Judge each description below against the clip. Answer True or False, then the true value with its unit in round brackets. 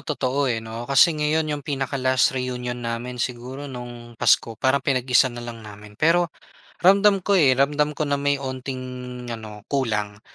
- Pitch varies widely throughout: False (3.2 semitones)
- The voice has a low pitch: True (130 Hz)